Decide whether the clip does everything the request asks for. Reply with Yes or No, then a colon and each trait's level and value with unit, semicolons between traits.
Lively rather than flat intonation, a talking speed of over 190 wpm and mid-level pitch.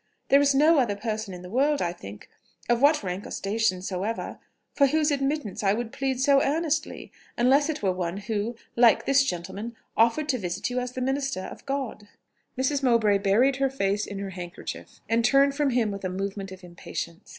No: wide, 5.8 semitones; average, 200 wpm; high, 235 Hz